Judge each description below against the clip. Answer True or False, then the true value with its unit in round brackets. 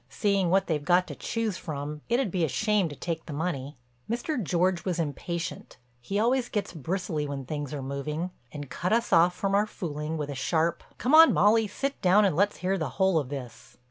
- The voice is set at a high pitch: False (175 Hz)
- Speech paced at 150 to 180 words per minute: False (205 wpm)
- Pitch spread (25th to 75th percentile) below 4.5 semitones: False (5.2 semitones)